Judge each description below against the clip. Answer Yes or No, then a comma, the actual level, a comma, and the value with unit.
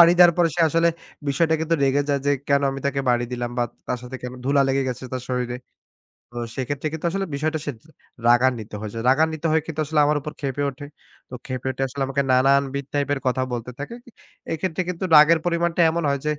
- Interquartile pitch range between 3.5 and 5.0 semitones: Yes, average, 3.8 semitones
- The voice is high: No, medium, 140 Hz